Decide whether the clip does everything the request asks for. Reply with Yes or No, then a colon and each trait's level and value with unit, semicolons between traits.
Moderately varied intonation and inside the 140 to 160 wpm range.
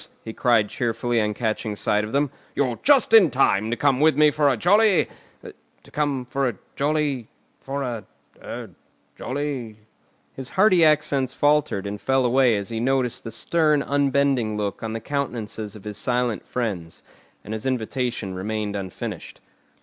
Yes: average, 4.7 semitones; average, 150 wpm